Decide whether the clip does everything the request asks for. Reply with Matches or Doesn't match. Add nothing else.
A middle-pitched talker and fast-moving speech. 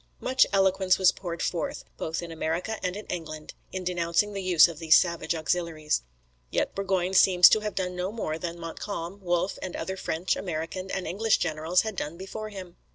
Doesn't match